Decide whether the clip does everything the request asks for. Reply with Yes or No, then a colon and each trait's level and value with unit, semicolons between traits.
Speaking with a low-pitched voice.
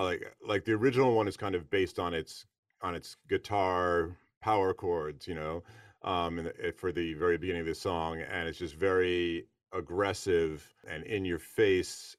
Yes: very low, 90 Hz